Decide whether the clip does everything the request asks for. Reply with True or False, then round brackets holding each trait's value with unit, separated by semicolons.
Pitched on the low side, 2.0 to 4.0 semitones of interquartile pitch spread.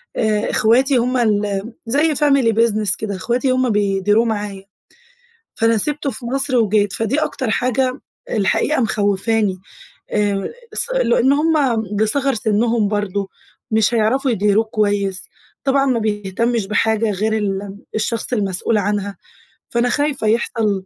False (220 Hz; 3.4 semitones)